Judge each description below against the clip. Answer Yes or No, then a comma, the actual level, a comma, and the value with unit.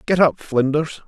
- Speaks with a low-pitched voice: No, medium, 145 Hz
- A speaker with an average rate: Yes, average, 170 wpm